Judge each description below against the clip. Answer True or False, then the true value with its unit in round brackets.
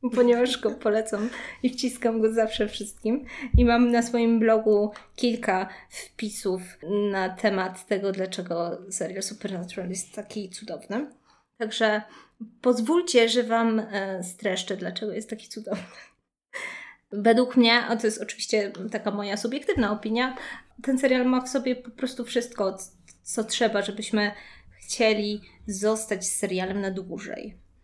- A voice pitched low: False (215 Hz)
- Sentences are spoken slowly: False (125 wpm)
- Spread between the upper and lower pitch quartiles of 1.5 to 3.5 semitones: True (2.9 semitones)